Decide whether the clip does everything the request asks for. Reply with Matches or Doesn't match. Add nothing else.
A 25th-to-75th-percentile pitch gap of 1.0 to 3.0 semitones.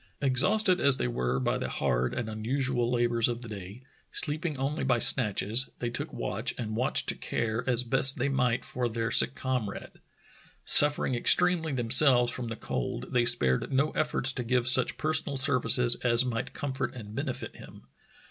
Matches